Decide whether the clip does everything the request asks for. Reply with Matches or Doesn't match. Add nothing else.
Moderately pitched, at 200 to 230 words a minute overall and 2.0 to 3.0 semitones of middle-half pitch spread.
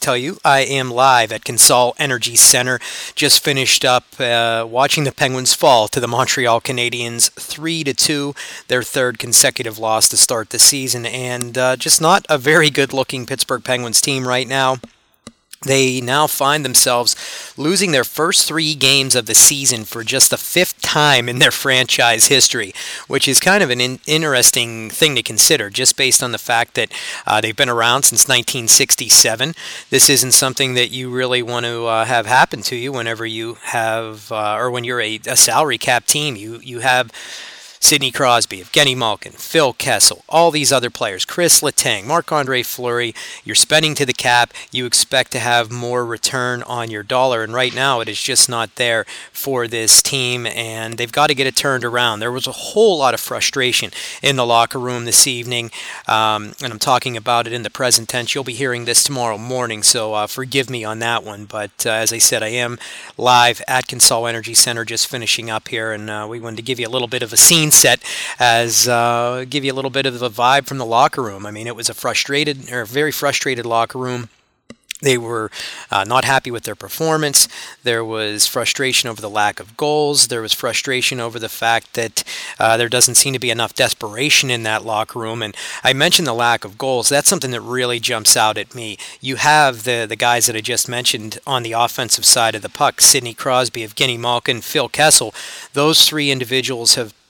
Doesn't match